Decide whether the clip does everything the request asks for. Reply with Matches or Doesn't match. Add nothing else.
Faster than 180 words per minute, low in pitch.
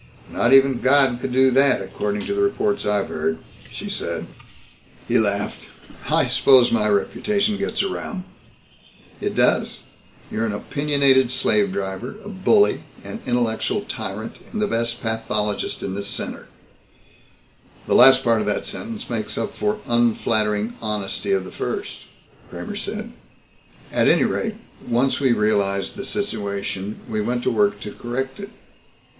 Doesn't match